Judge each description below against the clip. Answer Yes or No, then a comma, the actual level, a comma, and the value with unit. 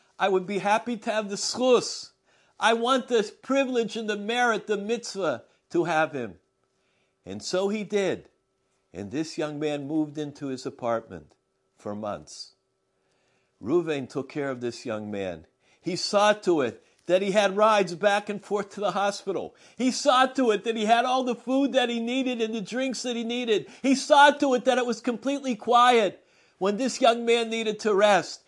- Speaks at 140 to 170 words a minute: No, average, 190 wpm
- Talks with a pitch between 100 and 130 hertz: No, high, 210 Hz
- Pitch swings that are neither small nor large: No, wide, 7.3 semitones